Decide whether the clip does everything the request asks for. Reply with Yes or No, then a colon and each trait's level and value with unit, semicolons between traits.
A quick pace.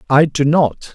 No: average, 190 wpm